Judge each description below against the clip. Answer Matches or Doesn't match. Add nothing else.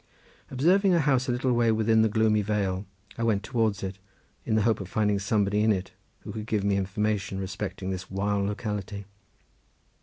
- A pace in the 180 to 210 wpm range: Matches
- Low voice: Matches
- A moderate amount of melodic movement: Doesn't match